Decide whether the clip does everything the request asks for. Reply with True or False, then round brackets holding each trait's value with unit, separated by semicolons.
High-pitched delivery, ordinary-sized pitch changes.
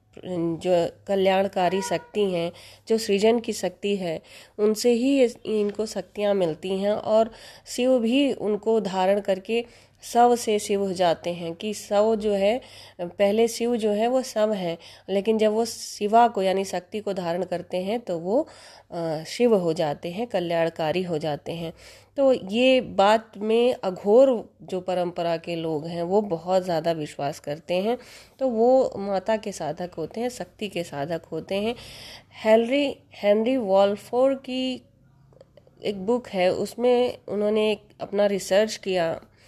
True (200 Hz; 4.2 semitones)